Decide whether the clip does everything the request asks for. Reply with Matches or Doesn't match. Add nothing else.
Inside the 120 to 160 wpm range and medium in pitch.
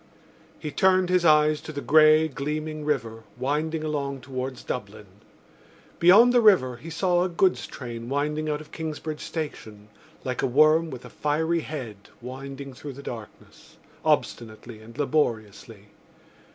Matches